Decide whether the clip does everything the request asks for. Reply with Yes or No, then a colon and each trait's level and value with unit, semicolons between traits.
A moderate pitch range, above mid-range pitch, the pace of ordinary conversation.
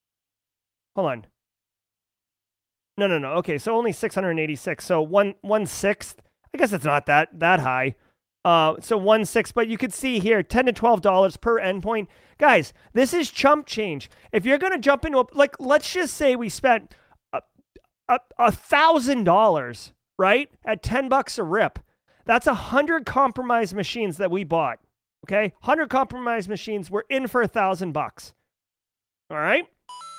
No: wide, 8.6 semitones; high, 215 Hz; average, 165 wpm